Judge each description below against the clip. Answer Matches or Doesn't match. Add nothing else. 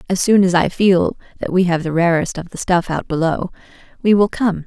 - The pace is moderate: Doesn't match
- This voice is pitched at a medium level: Matches